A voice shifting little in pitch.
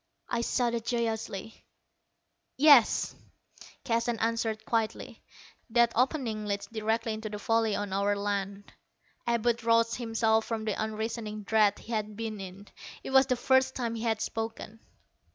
Yes: narrow, 1.6 semitones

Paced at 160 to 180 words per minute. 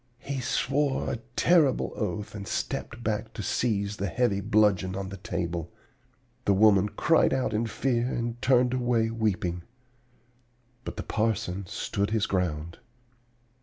No: average, 140 wpm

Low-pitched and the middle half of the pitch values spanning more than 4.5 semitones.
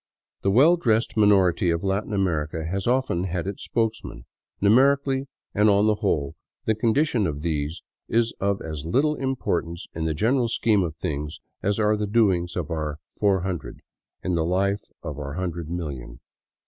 Yes: very low, 95 Hz; average, 5.2 semitones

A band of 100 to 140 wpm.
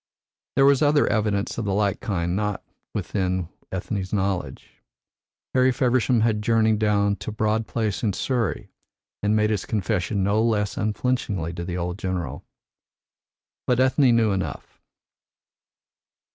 Yes: slow, 135 wpm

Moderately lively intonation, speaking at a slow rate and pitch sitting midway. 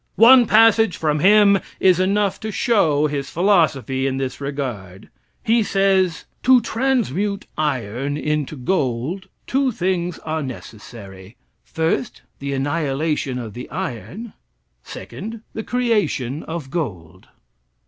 No: wide, 7.3 semitones; slow, 120 wpm; medium, 160 Hz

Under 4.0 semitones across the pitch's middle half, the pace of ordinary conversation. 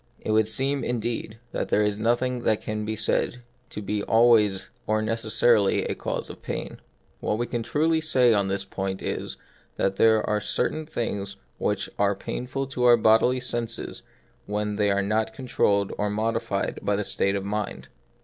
Yes: narrow, 2.6 semitones; average, 180 wpm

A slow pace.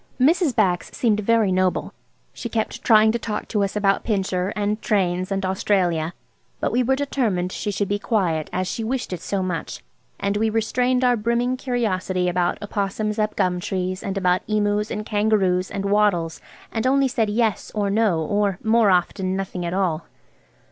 No: average, 180 wpm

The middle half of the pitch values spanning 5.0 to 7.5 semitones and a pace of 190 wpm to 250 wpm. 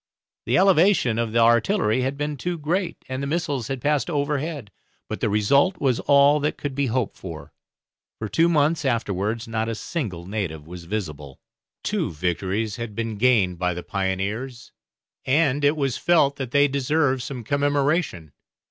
No: wide, 5.5 semitones; average, 165 wpm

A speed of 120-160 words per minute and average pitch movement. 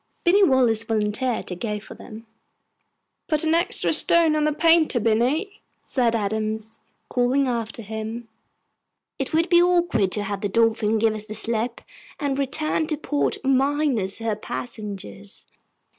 No: average, 145 wpm; wide, 5.7 semitones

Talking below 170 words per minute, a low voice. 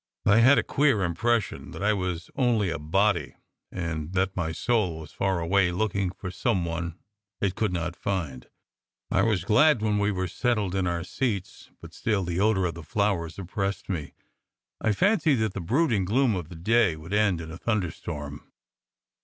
No: average, 185 wpm; very low, 95 Hz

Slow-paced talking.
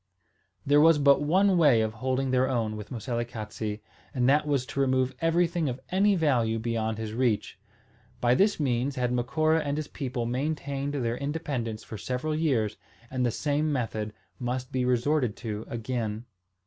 No: average, 165 wpm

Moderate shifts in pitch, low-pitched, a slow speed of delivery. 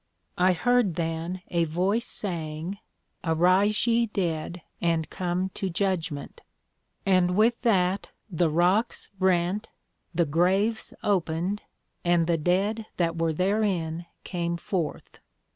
No: average, 3.1 semitones; medium, 180 Hz; slow, 115 wpm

